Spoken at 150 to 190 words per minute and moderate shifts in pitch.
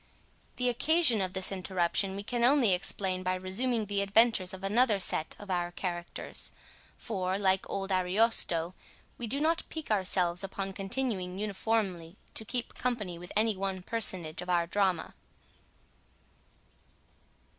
No: average, 140 wpm; average, 3.6 semitones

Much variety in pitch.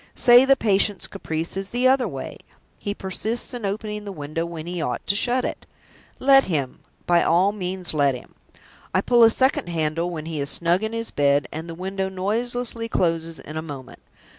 Yes: wide, 5.7 semitones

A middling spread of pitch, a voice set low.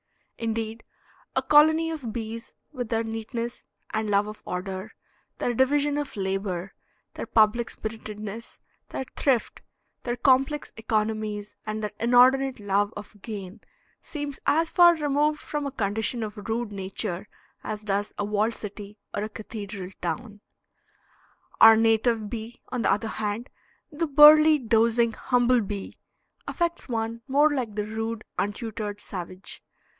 No: average, 3.5 semitones; high, 225 Hz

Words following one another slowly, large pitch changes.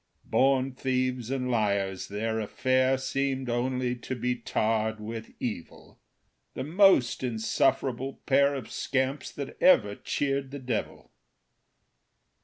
No: slow, 115 wpm; average, 3.0 semitones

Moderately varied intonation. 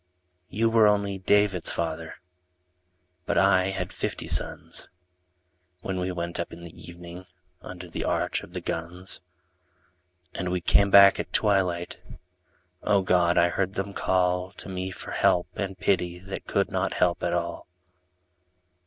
No: narrow, 1.9 semitones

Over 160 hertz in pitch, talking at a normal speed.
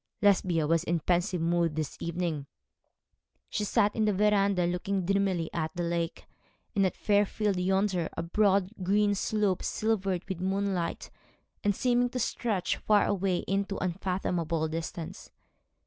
Yes: high, 190 Hz; average, 145 wpm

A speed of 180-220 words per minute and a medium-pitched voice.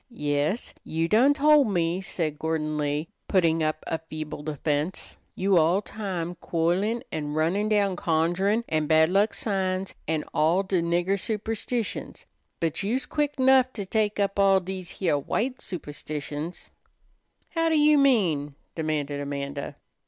No: average, 140 wpm; medium, 175 Hz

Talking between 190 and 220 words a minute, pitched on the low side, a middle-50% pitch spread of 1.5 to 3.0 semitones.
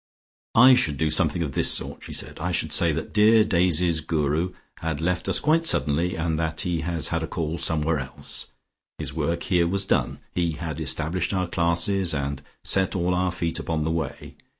Yes: average, 195 wpm; very low, 85 Hz; narrow, 2.4 semitones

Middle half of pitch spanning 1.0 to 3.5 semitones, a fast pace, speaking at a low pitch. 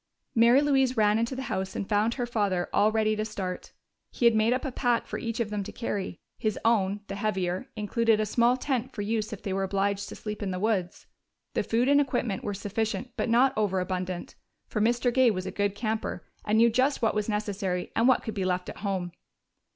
No: average, 3.0 semitones; fast, 225 wpm; high, 215 Hz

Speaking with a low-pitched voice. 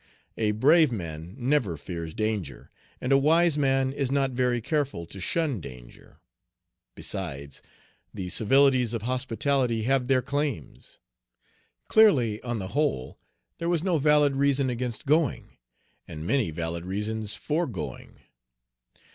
Yes: low, 125 Hz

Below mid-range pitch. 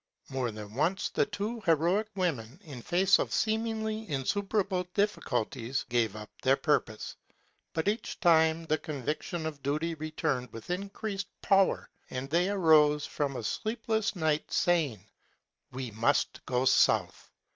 No: medium, 160 Hz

